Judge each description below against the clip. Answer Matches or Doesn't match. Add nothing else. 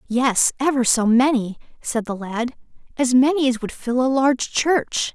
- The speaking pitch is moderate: Doesn't match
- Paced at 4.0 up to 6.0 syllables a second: Matches